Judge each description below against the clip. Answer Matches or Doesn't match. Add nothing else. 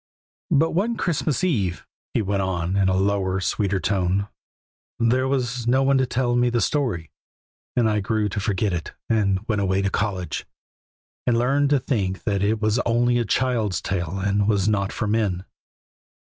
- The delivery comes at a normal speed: Matches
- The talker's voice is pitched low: Matches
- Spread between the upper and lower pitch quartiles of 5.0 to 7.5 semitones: Doesn't match